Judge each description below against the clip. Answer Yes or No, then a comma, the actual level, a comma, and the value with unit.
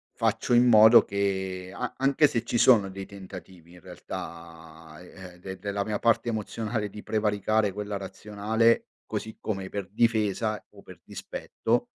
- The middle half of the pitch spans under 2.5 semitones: No, average, 2.8 semitones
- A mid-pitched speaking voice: No, low, 105 Hz